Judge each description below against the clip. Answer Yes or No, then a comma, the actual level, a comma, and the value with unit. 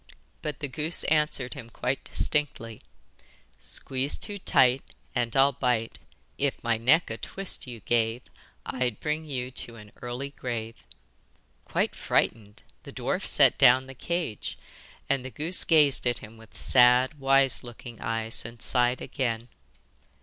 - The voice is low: Yes, low, 125 Hz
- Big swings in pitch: No, average, 3.2 semitones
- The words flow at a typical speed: Yes, average, 145 wpm